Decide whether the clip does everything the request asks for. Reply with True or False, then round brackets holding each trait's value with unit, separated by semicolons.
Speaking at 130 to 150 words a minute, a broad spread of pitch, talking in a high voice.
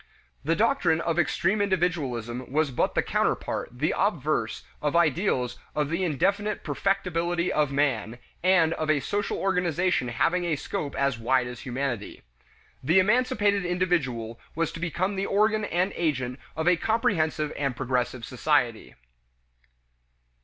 False (140 wpm; 5.9 semitones; 165 Hz)